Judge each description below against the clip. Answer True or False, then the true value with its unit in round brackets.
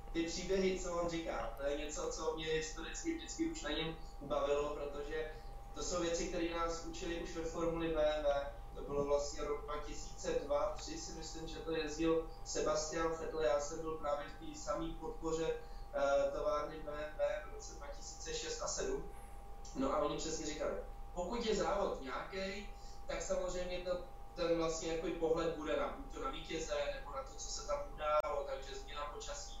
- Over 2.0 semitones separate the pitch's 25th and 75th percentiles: True (2.6 semitones)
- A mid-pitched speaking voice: True (160 Hz)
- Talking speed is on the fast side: True (175 wpm)